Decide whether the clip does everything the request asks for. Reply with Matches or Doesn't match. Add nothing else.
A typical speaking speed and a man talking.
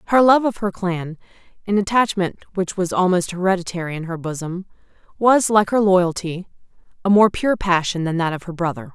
Doesn't match